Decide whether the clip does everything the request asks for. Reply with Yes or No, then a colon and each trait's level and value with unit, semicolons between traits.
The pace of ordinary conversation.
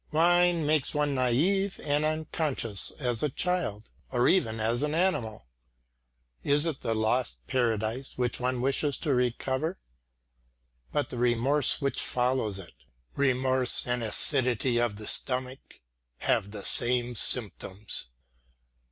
No: slow, 125 wpm